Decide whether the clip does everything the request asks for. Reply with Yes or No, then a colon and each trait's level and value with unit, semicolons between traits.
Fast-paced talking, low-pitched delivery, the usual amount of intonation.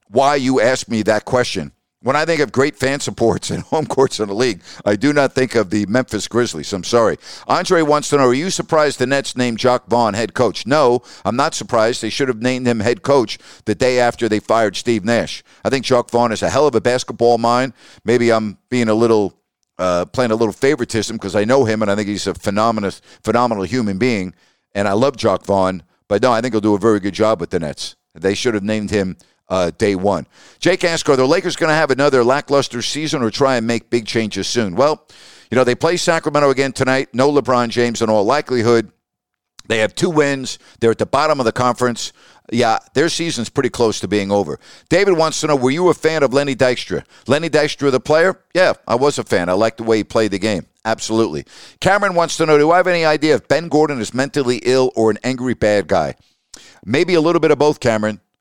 Yes: fast, 235 wpm; low, 120 Hz; average, 4.4 semitones